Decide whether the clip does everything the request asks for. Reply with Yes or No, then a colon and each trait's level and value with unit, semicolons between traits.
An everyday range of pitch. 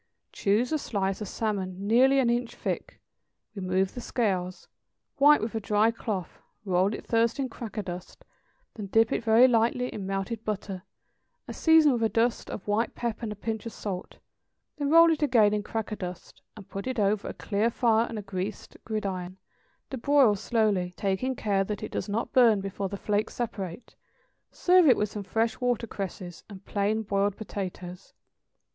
Yes: average, 3.2 semitones